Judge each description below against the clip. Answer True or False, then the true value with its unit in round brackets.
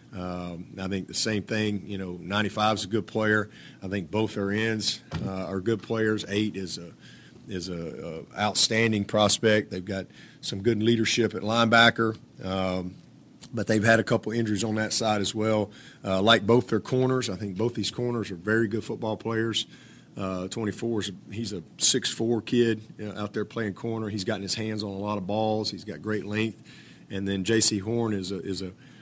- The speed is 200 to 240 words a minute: True (205 wpm)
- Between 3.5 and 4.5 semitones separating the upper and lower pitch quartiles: False (2.4 semitones)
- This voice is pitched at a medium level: False (110 Hz)